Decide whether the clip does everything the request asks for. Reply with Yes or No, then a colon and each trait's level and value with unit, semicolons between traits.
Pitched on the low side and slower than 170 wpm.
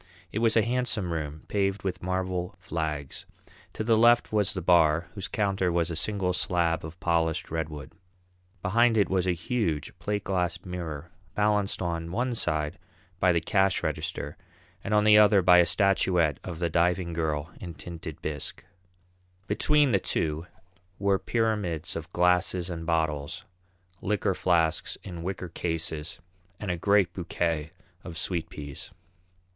Yes: very low, 90 Hz; average, 150 wpm